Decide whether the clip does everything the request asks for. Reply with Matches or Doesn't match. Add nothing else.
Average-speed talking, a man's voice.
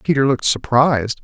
Matches